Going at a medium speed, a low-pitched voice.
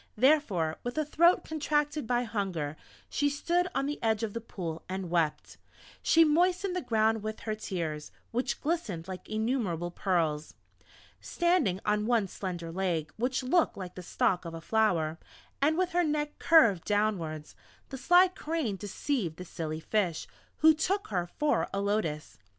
No: average, 160 wpm; high, 215 Hz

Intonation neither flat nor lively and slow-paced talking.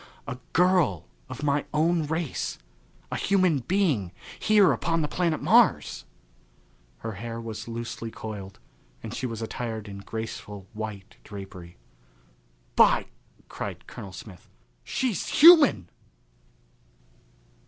No: wide, 8.3 semitones; slow, 115 wpm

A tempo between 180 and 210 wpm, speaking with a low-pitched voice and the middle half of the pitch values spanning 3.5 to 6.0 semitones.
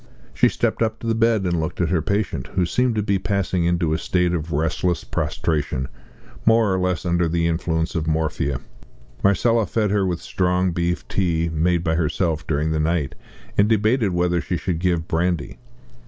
No: average, 185 wpm; very low, 85 Hz; average, 3.1 semitones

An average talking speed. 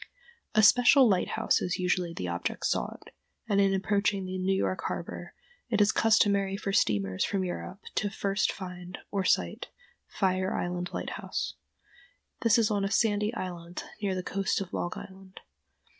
Yes: average, 155 wpm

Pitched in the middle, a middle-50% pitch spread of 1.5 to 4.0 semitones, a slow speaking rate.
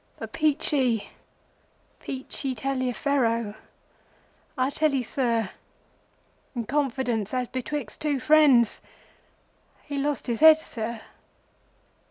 No: very high, 260 Hz; average, 3.5 semitones; slow, 95 wpm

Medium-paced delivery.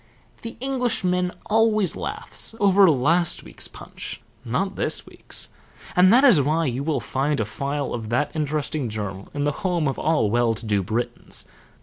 Yes: average, 165 wpm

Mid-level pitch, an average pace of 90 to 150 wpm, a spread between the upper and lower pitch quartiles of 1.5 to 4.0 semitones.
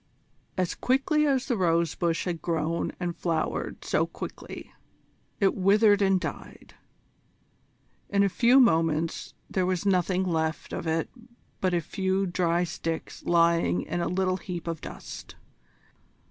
Yes: medium, 180 Hz; average, 140 wpm; average, 2.7 semitones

